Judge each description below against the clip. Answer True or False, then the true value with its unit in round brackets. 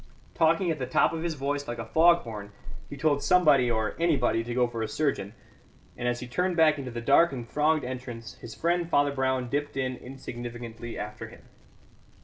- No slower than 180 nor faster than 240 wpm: True (200 wpm)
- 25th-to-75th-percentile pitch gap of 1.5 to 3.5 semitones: False (4.5 semitones)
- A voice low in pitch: True (130 Hz)